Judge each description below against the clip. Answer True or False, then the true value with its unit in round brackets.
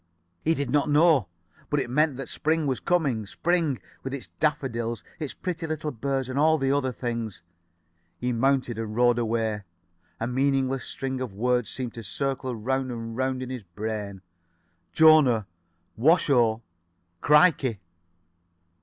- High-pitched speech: False (130 Hz)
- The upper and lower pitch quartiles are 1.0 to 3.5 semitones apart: False (3.9 semitones)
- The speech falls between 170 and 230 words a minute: False (150 wpm)